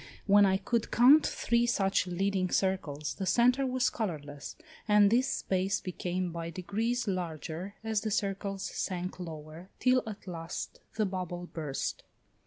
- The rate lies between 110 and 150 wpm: Yes, average, 145 wpm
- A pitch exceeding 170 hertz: Yes, high, 190 Hz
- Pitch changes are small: No, average, 3.6 semitones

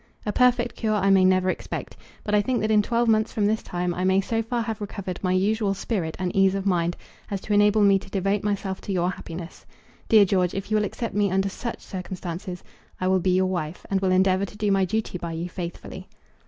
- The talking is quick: Yes, fast, 235 wpm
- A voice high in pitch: Yes, high, 195 Hz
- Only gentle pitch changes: Yes, narrow, 2.3 semitones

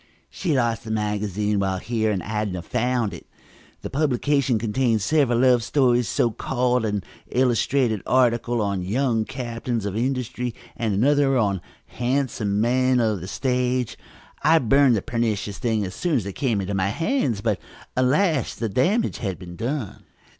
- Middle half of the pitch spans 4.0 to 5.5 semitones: No, average, 3.5 semitones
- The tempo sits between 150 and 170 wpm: Yes, average, 160 wpm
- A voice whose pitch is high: No, low, 120 Hz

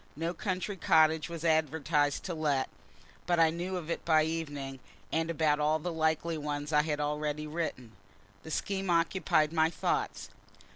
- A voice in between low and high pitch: Yes, medium, 160 Hz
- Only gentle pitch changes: Yes, narrow, 2.0 semitones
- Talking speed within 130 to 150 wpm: No, average, 160 wpm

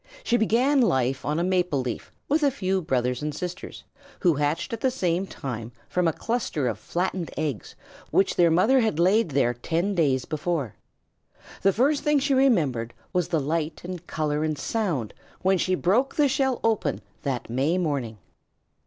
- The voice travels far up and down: Yes, wide, 7.1 semitones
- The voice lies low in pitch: No, medium, 175 Hz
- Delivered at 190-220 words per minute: No, average, 175 wpm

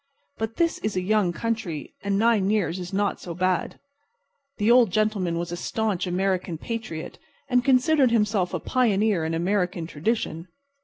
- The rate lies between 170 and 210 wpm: No, average, 160 wpm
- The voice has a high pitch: Yes, high, 200 Hz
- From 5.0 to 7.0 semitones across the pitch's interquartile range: No, average, 4.0 semitones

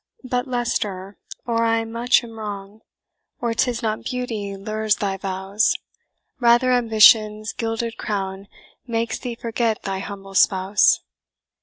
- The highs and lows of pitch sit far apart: No, average, 2.8 semitones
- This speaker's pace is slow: Yes, slow, 125 wpm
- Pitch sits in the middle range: No, high, 220 Hz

